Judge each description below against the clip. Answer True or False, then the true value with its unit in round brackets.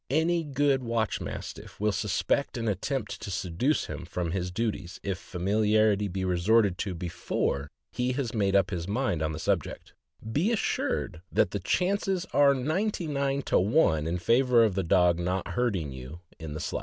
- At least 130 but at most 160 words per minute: False (180 wpm)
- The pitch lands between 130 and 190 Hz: False (105 Hz)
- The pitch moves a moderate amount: False (7.0 semitones)